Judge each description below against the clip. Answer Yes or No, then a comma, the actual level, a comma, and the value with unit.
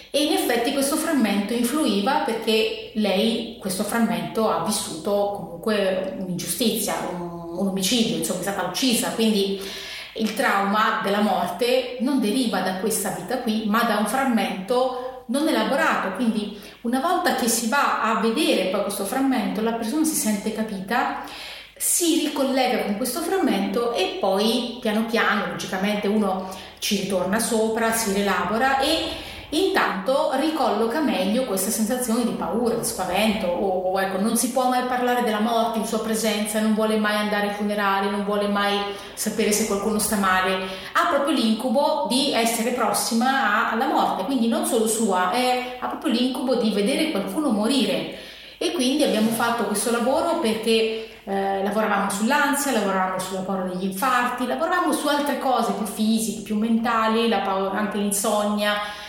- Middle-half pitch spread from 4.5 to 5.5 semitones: No, average, 3.8 semitones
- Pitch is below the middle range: No, high, 220 Hz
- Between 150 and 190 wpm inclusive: Yes, average, 155 wpm